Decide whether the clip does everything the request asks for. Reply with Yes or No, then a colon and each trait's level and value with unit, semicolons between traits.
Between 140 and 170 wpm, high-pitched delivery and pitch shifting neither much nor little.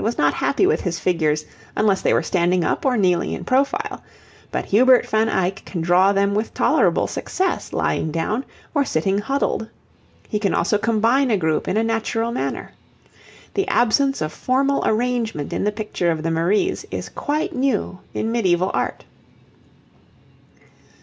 No: average, 165 wpm; high, 215 Hz; wide, 5.7 semitones